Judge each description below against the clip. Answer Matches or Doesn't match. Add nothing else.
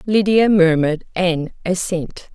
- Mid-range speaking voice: Matches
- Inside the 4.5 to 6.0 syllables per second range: Doesn't match